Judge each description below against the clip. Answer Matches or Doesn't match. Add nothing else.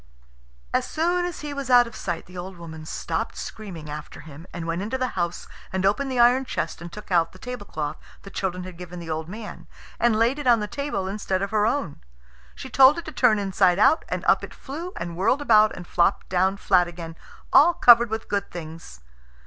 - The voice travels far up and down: Matches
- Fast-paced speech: Matches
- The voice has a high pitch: Matches